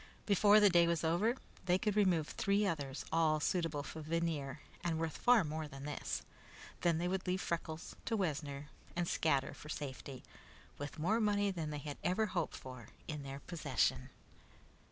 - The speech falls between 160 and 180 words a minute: Yes, average, 175 wpm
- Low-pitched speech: No, medium, 165 Hz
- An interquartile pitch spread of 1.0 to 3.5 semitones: No, average, 3.9 semitones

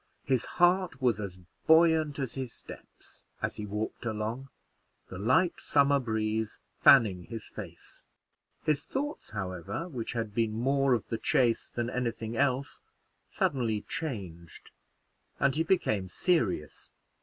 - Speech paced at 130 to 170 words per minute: Yes, slow, 135 wpm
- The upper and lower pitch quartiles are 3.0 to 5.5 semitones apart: Yes, average, 4.7 semitones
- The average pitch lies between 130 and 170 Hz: No, low, 120 Hz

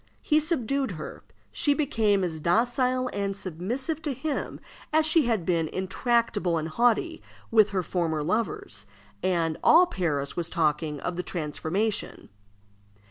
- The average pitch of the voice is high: Yes, high, 200 Hz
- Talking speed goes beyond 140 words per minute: No, slow, 135 wpm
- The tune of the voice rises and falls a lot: Yes, wide, 7.3 semitones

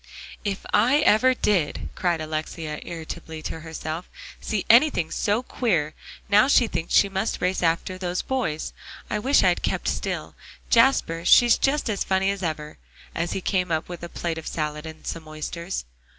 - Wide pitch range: No, average, 4.7 semitones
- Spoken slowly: No, average, 170 wpm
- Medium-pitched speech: Yes, medium, 175 Hz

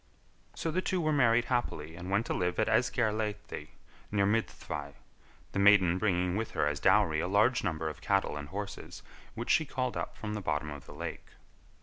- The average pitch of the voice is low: Yes, low, 100 Hz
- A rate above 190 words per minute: Yes, average, 200 wpm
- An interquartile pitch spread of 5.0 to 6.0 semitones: Yes, average, 5.3 semitones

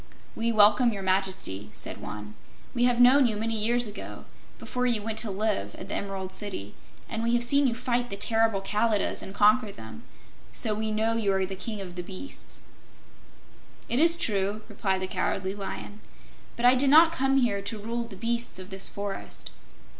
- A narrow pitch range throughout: No, average, 3.5 semitones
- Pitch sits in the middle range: No, high, 215 Hz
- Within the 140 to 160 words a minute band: No, average, 190 wpm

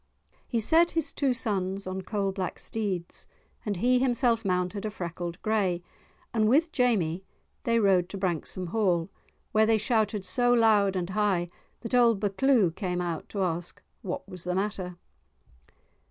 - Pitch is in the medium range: No, high, 200 Hz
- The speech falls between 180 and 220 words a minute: No, average, 155 wpm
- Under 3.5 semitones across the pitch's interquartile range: No, average, 3.9 semitones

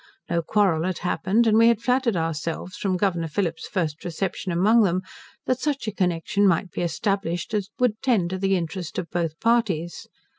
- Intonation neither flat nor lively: Yes, average, 4.1 semitones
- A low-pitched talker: No, medium, 185 Hz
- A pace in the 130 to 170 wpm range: No, average, 185 wpm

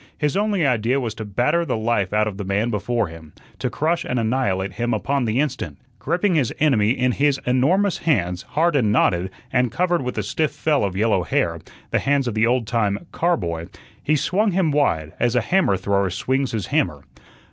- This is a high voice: No, low, 120 Hz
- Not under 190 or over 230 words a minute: Yes, fast, 205 wpm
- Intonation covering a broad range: Yes, wide, 6.5 semitones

